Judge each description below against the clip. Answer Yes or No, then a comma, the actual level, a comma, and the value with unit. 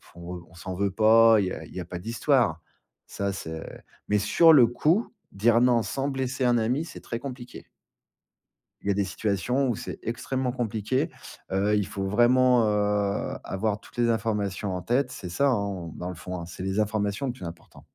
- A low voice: Yes, low, 105 Hz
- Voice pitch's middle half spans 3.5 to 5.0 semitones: Yes, average, 4.2 semitones